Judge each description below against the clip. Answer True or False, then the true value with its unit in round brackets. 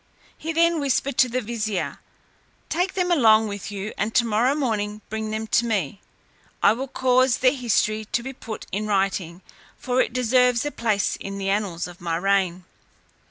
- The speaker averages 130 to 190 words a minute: True (175 wpm)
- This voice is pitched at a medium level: False (220 Hz)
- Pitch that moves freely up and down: False (4.0 semitones)